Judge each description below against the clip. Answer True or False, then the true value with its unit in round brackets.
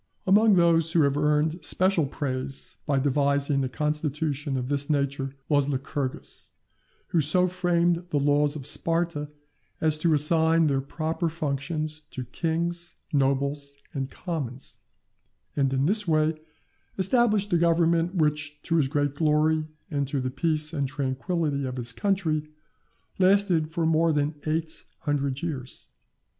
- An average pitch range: True (3.0 semitones)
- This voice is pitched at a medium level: True (150 Hz)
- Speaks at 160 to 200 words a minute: False (140 wpm)